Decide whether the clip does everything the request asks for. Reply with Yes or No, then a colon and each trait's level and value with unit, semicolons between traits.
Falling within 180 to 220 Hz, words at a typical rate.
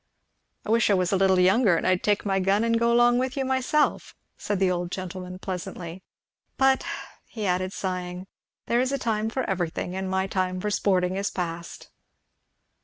Yes: high, 190 Hz; average, 185 wpm